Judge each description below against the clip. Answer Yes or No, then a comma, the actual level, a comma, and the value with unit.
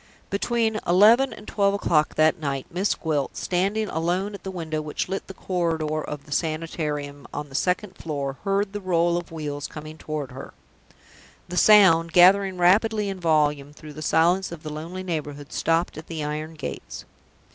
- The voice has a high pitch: No, medium, 165 Hz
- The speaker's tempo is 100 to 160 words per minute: No, average, 175 wpm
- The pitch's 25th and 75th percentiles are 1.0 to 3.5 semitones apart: No, average, 3.9 semitones